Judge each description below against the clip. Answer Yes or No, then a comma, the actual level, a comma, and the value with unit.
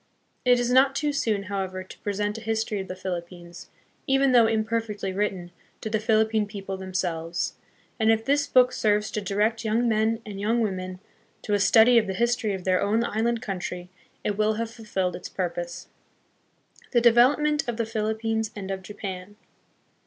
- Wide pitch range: No, average, 3.1 semitones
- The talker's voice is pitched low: No, high, 215 Hz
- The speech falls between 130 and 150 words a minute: No, average, 180 wpm